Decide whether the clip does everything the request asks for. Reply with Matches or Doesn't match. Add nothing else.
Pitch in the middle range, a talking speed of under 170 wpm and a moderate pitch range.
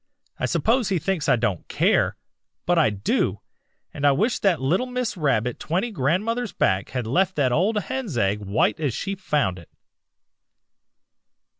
Doesn't match